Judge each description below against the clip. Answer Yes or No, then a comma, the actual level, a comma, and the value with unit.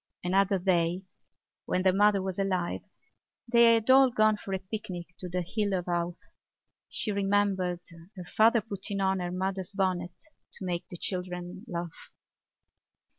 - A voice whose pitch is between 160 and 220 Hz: Yes, high, 190 Hz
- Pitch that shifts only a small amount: Yes, narrow, 2.3 semitones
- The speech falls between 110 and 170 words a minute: Yes, average, 150 wpm